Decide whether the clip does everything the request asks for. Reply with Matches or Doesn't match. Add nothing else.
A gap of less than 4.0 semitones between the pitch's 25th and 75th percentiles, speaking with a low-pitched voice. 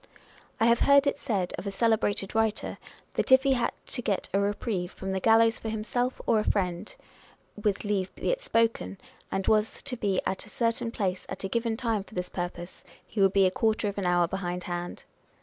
Doesn't match